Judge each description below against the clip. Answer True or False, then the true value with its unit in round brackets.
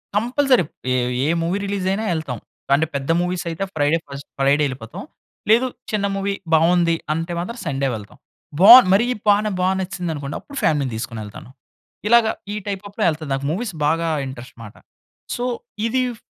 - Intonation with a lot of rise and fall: True (6.3 semitones)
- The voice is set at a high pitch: False (170 Hz)